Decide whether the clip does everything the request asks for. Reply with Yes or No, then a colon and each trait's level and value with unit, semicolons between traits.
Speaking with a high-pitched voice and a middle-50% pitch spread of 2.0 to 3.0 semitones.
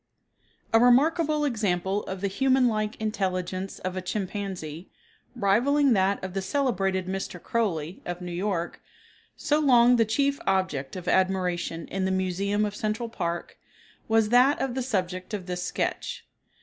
No: high, 195 Hz; average, 4.3 semitones